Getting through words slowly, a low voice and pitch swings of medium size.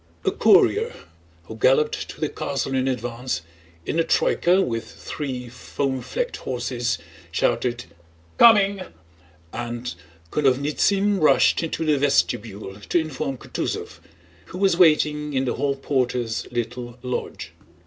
Yes: slow, 125 wpm; low, 130 Hz; average, 4.0 semitones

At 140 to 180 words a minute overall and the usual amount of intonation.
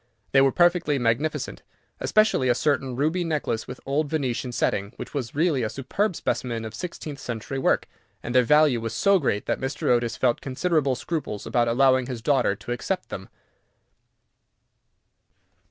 Yes: average, 160 wpm; average, 4.3 semitones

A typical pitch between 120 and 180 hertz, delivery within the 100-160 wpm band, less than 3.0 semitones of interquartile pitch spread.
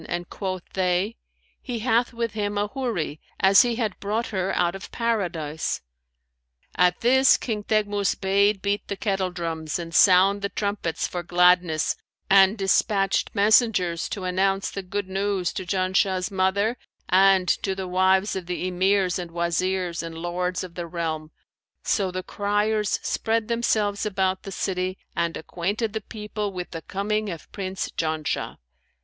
No: high, 190 Hz; average, 155 wpm; narrow, 2.5 semitones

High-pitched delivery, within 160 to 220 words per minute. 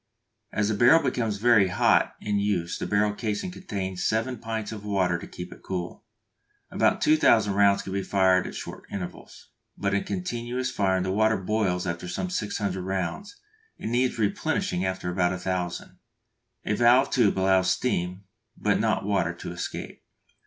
No: low, 100 Hz; average, 165 wpm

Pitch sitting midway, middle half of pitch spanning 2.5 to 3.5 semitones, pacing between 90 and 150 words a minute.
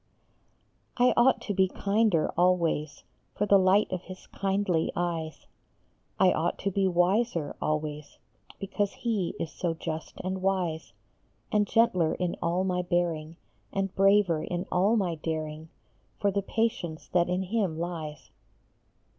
Yes: medium, 180 Hz; average, 3.2 semitones; average, 140 wpm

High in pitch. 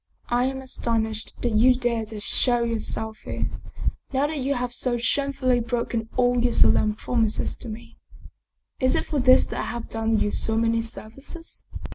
Yes: high, 240 Hz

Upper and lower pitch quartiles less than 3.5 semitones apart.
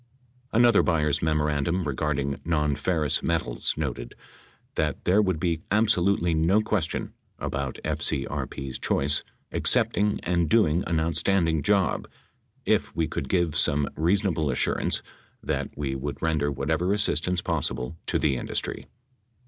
No: average, 4.0 semitones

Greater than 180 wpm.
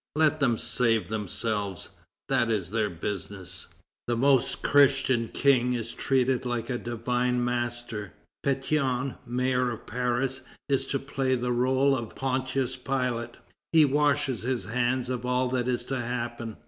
No: average, 145 wpm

